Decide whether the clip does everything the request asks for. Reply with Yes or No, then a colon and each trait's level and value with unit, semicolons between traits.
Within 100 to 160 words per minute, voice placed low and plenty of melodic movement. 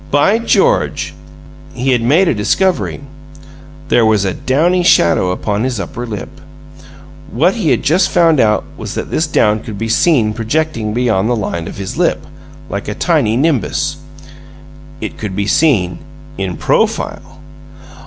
Yes: average, 155 wpm; low, 120 Hz; wide, 6.9 semitones